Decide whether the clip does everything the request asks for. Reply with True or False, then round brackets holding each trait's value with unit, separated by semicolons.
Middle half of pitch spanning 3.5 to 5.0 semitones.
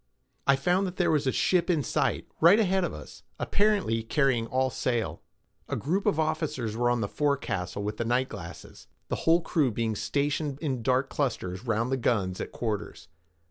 False (5.6 semitones)